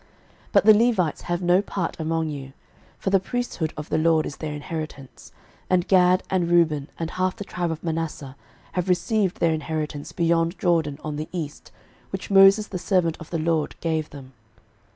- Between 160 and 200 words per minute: Yes, average, 185 wpm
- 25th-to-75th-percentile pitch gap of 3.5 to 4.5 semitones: No, average, 2.9 semitones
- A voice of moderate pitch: Yes, medium, 165 Hz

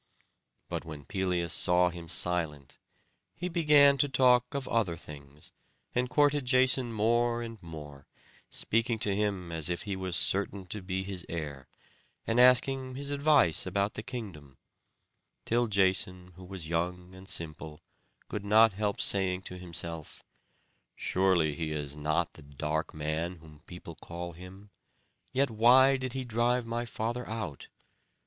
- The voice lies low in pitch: Yes, very low, 95 Hz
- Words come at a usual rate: Yes, average, 150 wpm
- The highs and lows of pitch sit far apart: Yes, wide, 6.2 semitones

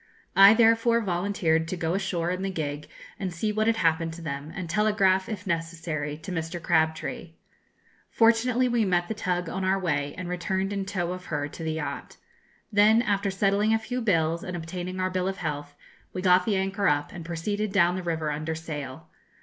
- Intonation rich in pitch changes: No, average, 3.7 semitones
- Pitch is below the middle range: No, medium, 180 Hz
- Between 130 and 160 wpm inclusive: No, average, 200 wpm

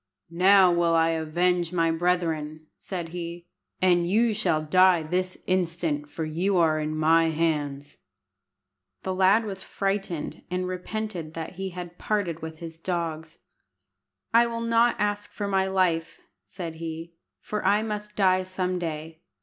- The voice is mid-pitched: Yes, medium, 175 Hz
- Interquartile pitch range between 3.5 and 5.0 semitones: No, average, 2.7 semitones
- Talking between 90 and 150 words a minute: Yes, average, 145 wpm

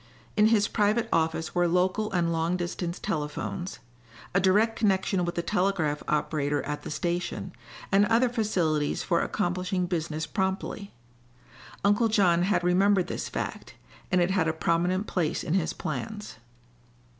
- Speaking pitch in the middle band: Yes, medium, 180 Hz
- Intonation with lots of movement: No, average, 3.3 semitones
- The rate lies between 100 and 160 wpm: Yes, average, 145 wpm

